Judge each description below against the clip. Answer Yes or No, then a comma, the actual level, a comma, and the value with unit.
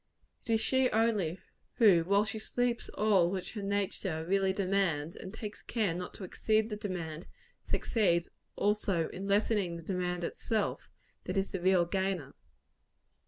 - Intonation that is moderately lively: Yes, average, 3.2 semitones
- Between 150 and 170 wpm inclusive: Yes, average, 155 wpm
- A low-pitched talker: No, high, 195 Hz